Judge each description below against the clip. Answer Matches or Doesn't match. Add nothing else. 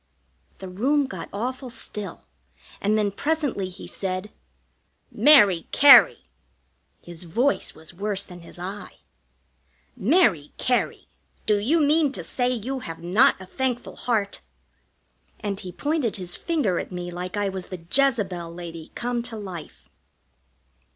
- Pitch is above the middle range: Matches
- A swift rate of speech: Doesn't match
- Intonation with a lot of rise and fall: Matches